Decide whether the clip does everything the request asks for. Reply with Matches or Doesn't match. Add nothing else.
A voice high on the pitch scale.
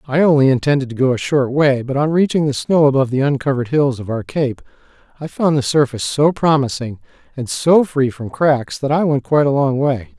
Doesn't match